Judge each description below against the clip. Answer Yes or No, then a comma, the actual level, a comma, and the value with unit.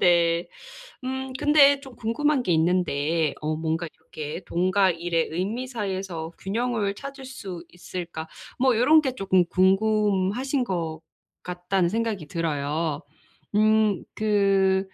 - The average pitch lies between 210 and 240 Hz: No, high, 190 Hz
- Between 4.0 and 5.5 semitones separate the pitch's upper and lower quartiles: Yes, average, 5.2 semitones